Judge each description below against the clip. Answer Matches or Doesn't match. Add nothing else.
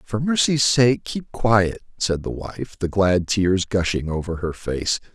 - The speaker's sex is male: Matches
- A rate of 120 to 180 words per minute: Matches